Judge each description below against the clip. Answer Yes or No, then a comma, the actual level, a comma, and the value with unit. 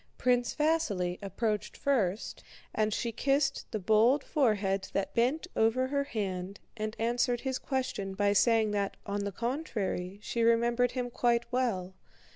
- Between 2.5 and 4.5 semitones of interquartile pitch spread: Yes, average, 3.9 semitones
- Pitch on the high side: Yes, high, 230 Hz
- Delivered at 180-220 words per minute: No, average, 145 wpm